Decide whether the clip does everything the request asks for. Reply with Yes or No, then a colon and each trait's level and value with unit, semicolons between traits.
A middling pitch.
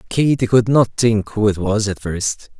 No: low, 110 Hz